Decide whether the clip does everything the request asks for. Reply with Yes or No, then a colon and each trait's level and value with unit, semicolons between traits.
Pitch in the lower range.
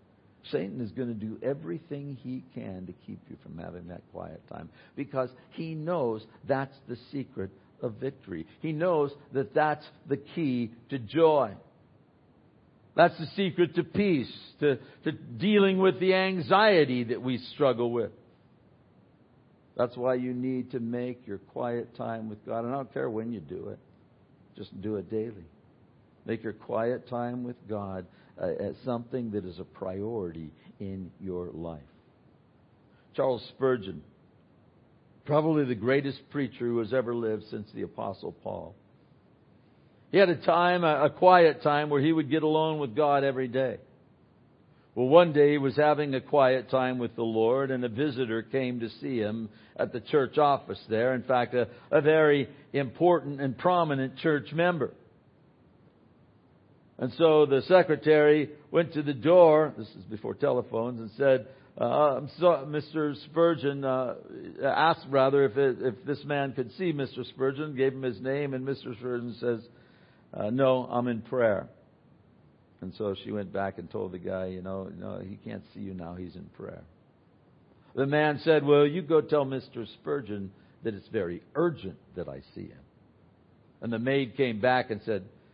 Yes: low, 130 Hz